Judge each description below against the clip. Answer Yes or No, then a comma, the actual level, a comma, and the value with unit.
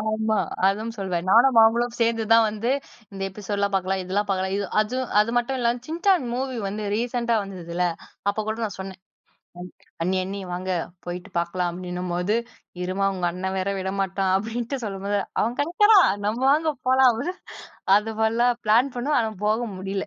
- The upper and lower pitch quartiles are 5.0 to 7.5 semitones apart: No, average, 3.7 semitones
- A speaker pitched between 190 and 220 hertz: Yes, high, 210 Hz